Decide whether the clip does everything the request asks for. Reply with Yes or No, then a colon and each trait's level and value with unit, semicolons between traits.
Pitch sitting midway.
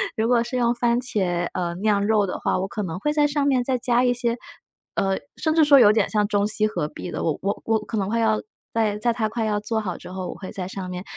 No: high, 215 Hz